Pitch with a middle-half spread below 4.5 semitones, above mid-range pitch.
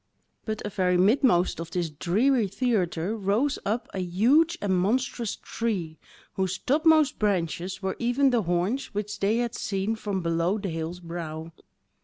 No: average, 5.0 semitones; high, 200 Hz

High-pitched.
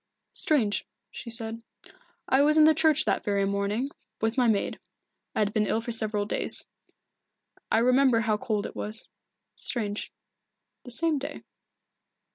Yes: high, 230 Hz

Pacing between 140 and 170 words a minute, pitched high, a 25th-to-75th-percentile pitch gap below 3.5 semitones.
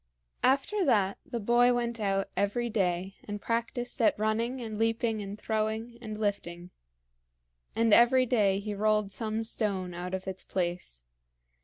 Yes: average, 150 wpm; high, 215 Hz; average, 3.1 semitones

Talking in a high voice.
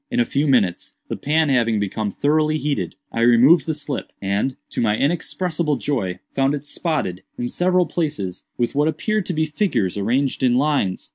No: medium, 140 Hz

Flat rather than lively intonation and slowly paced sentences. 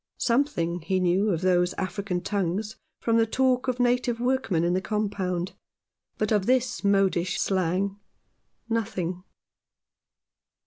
No: average, 4.1 semitones; slow, 125 wpm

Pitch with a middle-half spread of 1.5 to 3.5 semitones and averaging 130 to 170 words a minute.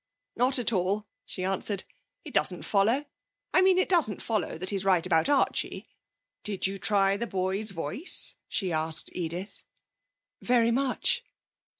No: average, 4.2 semitones; average, 145 wpm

